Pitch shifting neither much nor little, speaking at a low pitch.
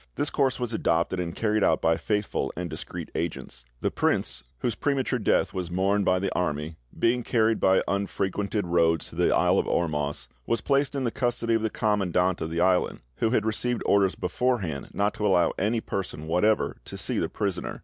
Yes: average, 4.4 semitones; low, 100 Hz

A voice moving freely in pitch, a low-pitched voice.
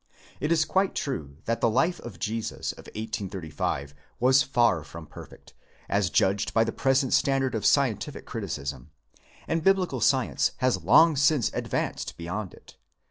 Yes: wide, 6.3 semitones; low, 115 Hz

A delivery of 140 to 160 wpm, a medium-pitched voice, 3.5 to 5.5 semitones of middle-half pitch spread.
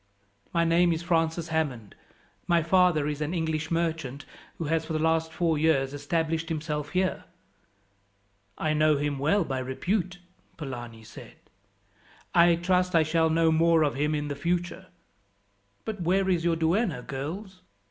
No: average, 155 wpm; medium, 160 Hz; narrow, 2.4 semitones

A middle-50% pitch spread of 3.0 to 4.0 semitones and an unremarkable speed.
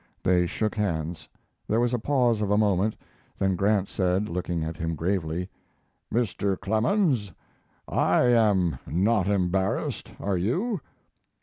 No: average, 3.7 semitones; slow, 130 wpm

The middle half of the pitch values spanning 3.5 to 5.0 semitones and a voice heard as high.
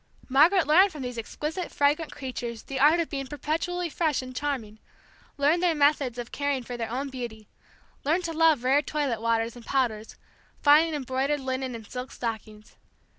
Yes: average, 3.9 semitones; very high, 275 Hz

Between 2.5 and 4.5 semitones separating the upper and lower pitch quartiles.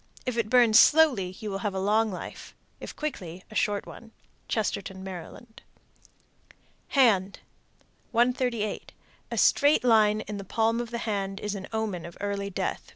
Yes: average, 3.2 semitones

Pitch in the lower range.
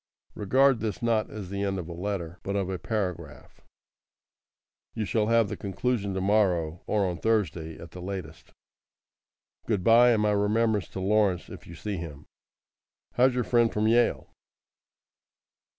Yes: low, 100 Hz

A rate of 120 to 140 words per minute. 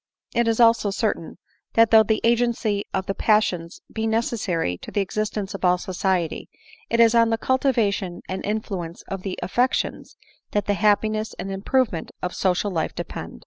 No: average, 180 wpm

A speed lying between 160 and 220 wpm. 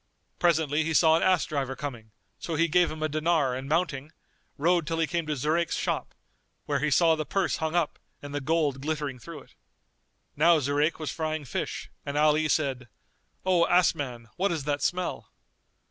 Yes: average, 190 wpm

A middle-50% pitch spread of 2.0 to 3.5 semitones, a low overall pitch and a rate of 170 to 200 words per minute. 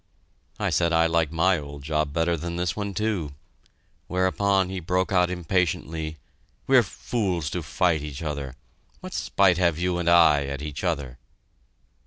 No: average, 3.2 semitones; very low, 85 Hz; average, 160 wpm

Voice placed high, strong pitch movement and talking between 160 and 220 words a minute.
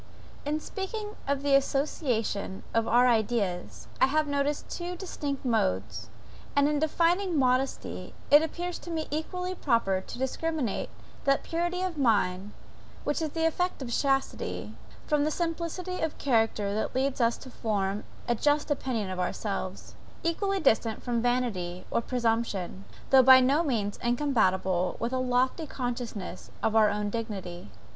No: very high, 255 Hz; wide, 6.0 semitones; average, 150 wpm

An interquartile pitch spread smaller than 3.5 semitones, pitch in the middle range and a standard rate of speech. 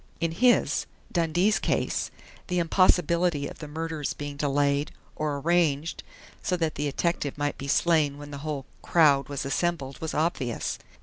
Yes: average, 3.1 semitones; medium, 150 Hz; average, 150 wpm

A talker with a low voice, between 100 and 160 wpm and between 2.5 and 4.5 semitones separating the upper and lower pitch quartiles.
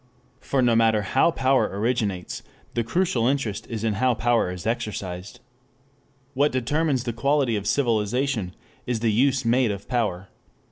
Yes: low, 120 Hz; average, 150 wpm; average, 3.7 semitones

